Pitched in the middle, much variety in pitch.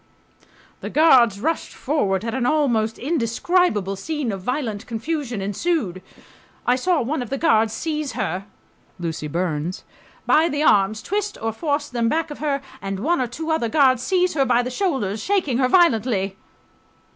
No: very high, 250 Hz; wide, 6.4 semitones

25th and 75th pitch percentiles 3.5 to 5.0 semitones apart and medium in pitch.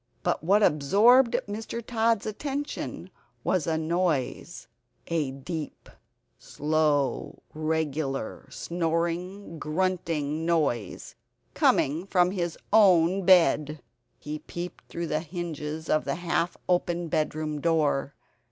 No: average, 3.0 semitones; medium, 165 Hz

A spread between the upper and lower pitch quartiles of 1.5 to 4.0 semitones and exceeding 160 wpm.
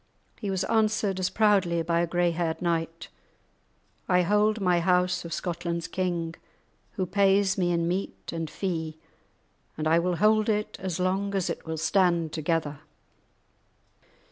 No: narrow, 2.6 semitones; average, 150 wpm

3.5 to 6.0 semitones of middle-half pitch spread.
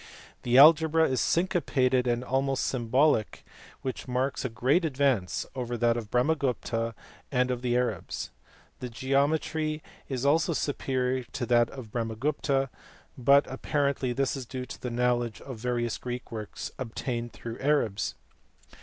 No: narrow, 2.6 semitones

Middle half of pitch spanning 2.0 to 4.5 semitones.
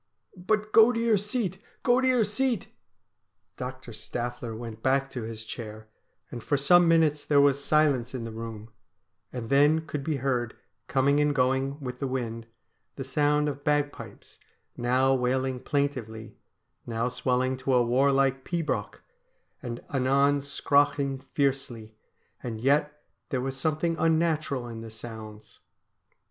Yes: average, 3.4 semitones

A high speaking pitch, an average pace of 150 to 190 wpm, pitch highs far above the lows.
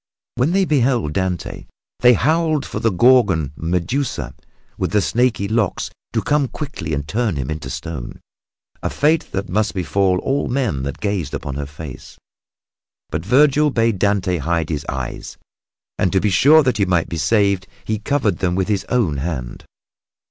No: low, 100 Hz; average, 170 wpm; wide, 7.3 semitones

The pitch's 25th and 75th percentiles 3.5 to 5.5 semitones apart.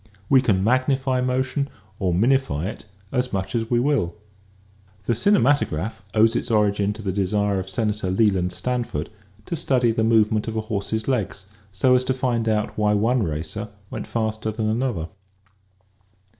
Yes: average, 3.9 semitones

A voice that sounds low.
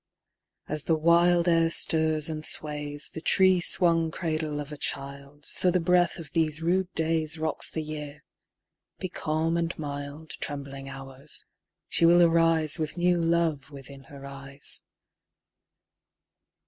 No: medium, 155 Hz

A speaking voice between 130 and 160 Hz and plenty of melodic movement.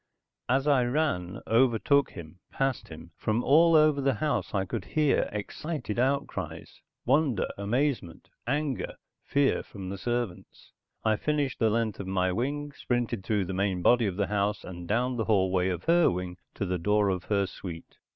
No: low, 110 Hz; wide, 6.3 semitones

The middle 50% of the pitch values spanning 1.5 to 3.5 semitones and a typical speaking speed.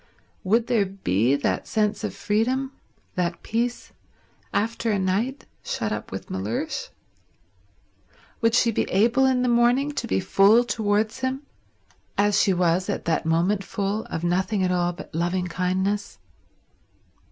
No: average, 4.5 semitones; average, 145 wpm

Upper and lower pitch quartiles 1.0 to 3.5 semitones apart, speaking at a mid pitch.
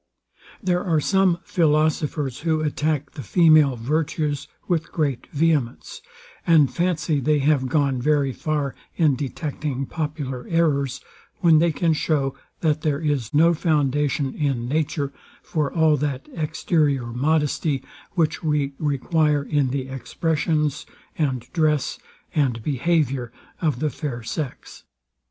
Yes: narrow, 2.5 semitones; medium, 150 Hz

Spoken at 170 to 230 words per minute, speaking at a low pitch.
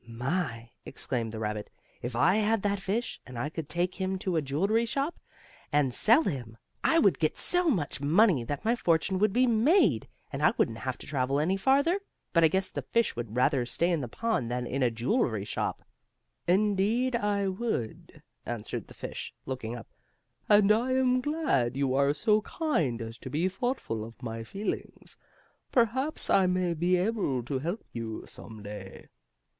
No: average, 180 wpm; medium, 170 Hz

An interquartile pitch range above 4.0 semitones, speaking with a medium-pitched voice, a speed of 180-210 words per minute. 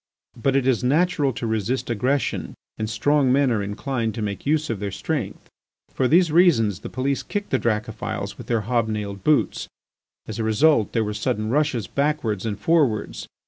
No: average, 4.8 semitones; low, 120 Hz; average, 185 wpm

